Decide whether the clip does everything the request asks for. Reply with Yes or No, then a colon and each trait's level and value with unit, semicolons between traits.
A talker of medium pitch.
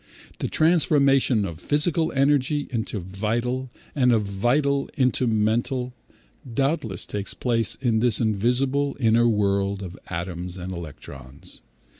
No: low, 115 Hz